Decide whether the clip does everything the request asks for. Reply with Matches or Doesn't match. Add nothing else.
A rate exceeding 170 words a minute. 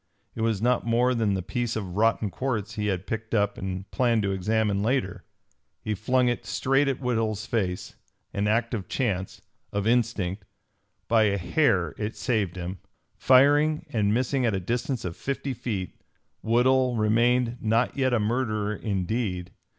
Doesn't match